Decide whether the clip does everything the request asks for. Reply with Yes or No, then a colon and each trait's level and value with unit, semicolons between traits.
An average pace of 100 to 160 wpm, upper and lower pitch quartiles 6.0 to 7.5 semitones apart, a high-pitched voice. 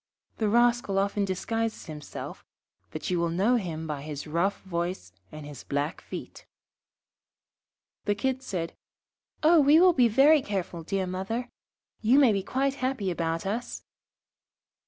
Yes: average, 145 wpm; wide, 6.3 semitones; high, 200 Hz